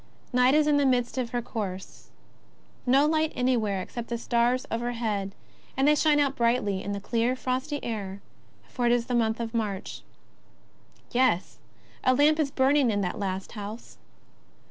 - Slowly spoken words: No, average, 165 wpm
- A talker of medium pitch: No, high, 240 Hz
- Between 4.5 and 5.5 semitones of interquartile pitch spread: No, average, 3.6 semitones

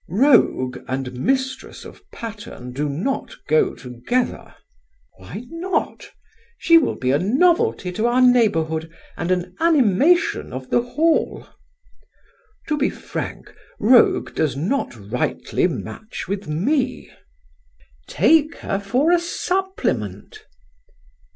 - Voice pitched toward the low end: No, high, 225 Hz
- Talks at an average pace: No, slow, 110 wpm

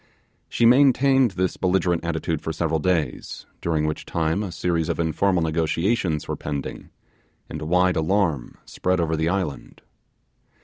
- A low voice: Yes, very low, 85 Hz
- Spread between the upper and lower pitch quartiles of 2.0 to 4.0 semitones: Yes, average, 2.8 semitones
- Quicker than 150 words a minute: No, average, 140 wpm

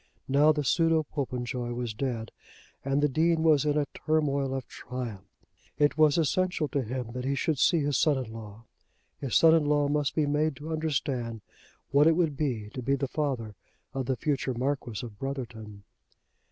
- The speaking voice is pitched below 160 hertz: Yes, medium, 140 Hz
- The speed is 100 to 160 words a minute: No, average, 185 wpm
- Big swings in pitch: No, average, 3.5 semitones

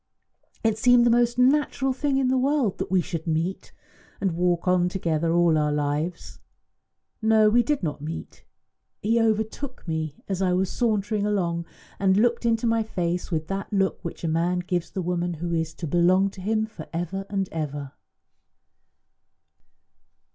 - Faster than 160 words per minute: Yes, average, 170 wpm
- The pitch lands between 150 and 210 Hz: Yes, high, 190 Hz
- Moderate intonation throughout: Yes, average, 4.7 semitones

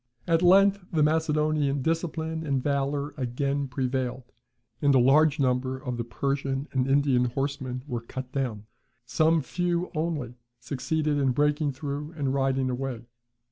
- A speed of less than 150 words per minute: Yes, average, 140 wpm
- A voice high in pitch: No, medium, 140 Hz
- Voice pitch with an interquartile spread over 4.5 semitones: No, average, 3.0 semitones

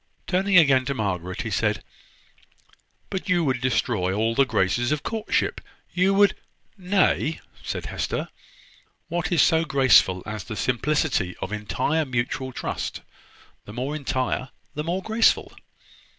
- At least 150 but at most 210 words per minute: No, average, 140 wpm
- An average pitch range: No, wide, 7.0 semitones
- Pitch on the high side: No, low, 135 Hz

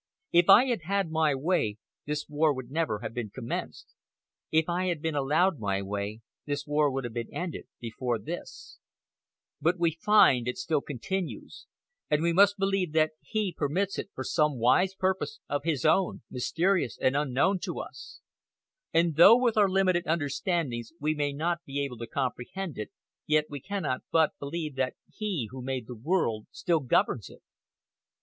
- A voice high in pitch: No, medium, 155 Hz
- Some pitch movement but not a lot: No, wide, 5.7 semitones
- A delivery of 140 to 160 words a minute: No, average, 175 wpm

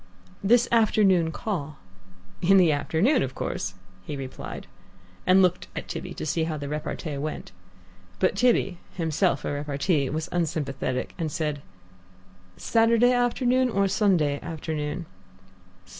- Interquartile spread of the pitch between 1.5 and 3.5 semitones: No, average, 5.1 semitones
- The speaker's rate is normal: No, slow, 130 wpm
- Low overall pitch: No, medium, 165 Hz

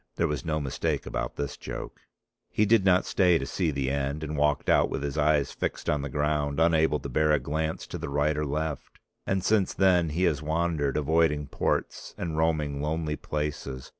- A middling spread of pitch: No, narrow, 2.1 semitones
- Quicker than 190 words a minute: Yes, average, 200 wpm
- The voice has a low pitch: Yes, very low, 75 Hz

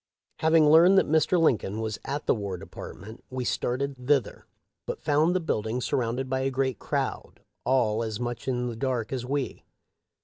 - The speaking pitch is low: Yes, low, 130 Hz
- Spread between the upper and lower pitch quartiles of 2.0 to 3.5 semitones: No, average, 3.9 semitones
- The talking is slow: No, average, 175 wpm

